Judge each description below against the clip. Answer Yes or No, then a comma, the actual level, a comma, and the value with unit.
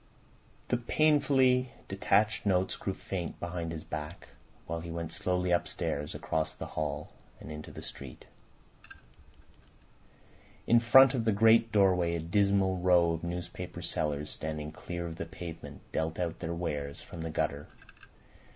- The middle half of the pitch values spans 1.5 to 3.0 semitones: No, average, 3.9 semitones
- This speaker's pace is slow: No, average, 145 wpm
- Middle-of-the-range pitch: No, very low, 85 Hz